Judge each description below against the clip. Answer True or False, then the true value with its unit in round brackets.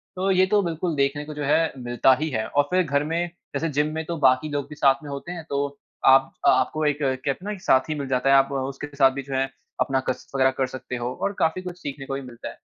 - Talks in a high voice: False (140 Hz)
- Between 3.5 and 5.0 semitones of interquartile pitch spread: False (2.8 semitones)